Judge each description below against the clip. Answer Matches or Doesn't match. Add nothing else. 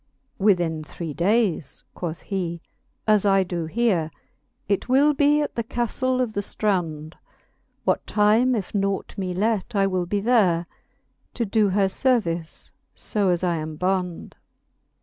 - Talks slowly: Doesn't match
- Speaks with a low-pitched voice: Doesn't match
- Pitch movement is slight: Doesn't match